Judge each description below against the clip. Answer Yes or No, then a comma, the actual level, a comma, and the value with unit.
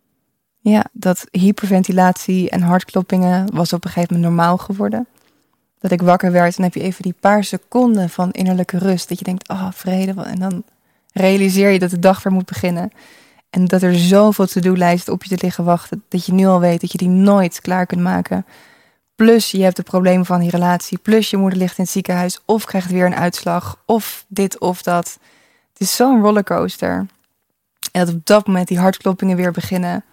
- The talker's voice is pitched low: No, medium, 185 Hz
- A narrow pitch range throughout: Yes, narrow, 1.6 semitones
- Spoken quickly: Yes, fast, 205 wpm